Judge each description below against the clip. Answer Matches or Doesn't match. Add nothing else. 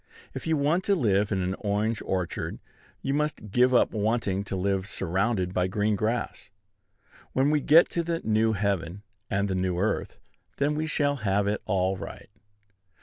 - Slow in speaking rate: Doesn't match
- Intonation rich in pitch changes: Matches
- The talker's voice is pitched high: Doesn't match